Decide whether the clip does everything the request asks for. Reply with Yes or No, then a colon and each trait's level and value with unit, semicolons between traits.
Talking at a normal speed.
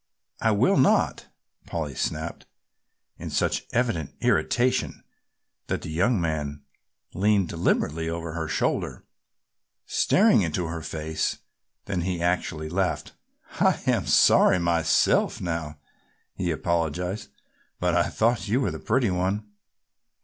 No: slow, 120 wpm